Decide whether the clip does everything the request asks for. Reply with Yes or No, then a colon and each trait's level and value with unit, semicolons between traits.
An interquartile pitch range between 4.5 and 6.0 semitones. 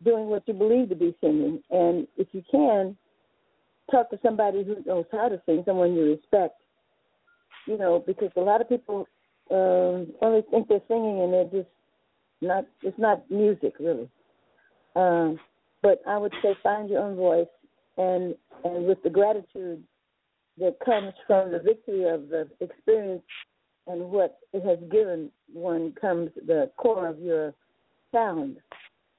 No: average, 3.6 semitones